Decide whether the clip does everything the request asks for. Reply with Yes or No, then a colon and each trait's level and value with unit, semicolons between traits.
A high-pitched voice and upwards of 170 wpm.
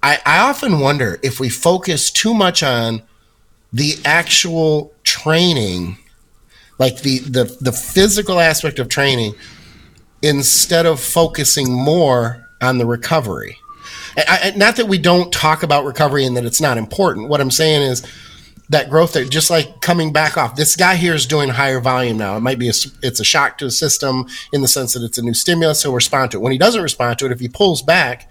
No: medium, 140 Hz; average, 195 wpm